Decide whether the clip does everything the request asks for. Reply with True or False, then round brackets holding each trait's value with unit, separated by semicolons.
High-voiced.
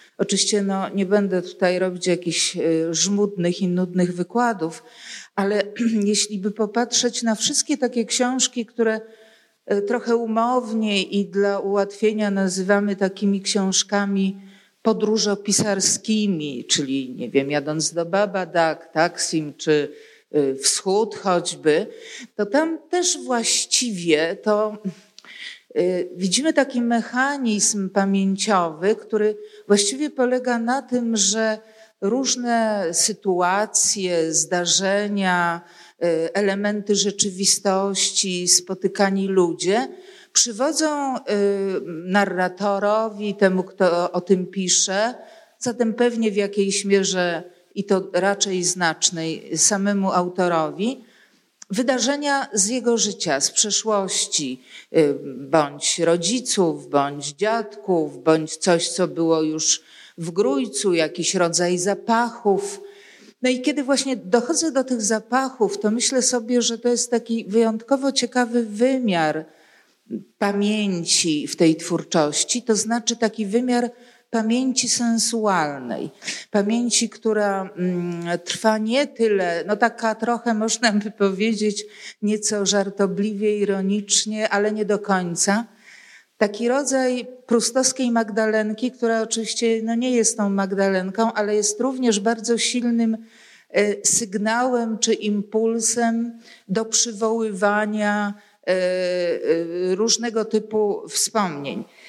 True (210 Hz)